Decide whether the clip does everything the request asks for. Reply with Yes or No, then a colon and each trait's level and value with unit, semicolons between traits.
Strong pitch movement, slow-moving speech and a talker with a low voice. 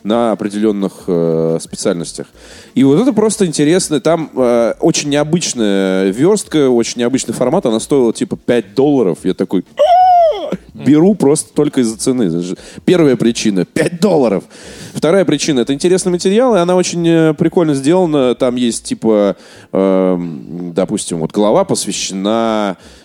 No: wide, 8.4 semitones; average, 130 wpm; low, 125 Hz